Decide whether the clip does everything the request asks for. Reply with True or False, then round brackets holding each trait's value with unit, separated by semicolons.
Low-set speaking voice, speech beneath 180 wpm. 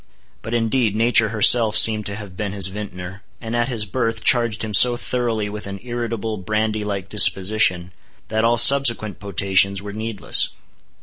True (110 Hz; 165 wpm)